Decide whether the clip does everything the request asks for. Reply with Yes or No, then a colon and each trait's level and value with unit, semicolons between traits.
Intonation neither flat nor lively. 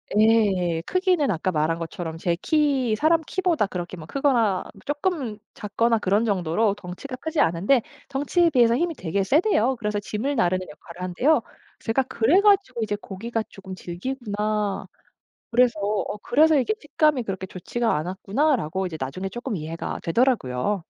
No: wide, 6.7 semitones